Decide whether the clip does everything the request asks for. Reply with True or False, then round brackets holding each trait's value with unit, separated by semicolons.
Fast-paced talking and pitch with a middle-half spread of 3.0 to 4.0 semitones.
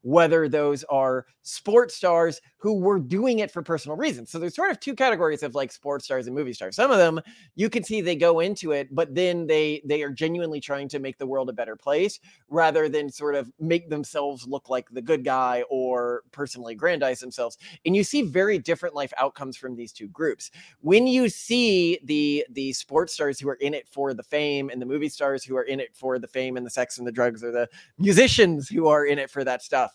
False (230 wpm; 4.5 semitones)